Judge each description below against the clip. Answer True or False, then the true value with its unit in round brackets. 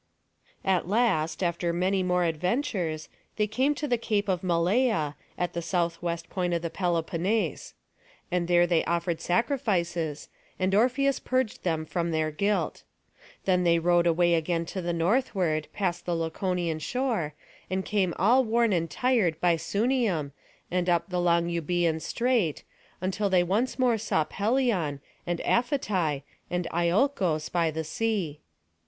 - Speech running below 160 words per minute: True (150 wpm)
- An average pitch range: True (4.0 semitones)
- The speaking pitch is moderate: True (180 Hz)